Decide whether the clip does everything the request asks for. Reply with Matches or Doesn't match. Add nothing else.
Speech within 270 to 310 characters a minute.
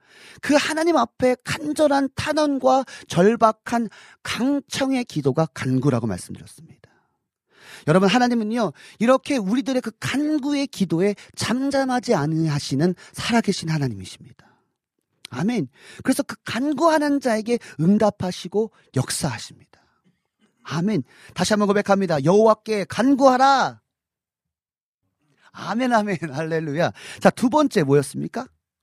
Matches